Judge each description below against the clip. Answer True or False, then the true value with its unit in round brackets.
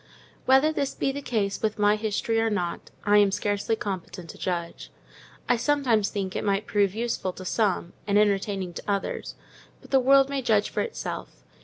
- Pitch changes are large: False (3.3 semitones)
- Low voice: False (210 Hz)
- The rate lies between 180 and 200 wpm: True (185 wpm)